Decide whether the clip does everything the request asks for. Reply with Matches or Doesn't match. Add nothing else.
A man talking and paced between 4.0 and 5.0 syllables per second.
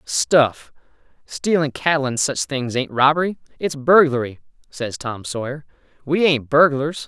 Matches